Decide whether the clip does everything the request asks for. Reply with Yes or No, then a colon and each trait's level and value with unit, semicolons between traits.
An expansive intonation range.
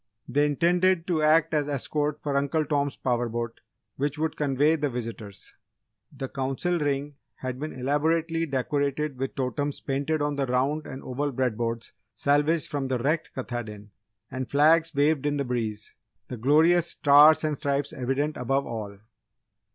No: average, 2.9 semitones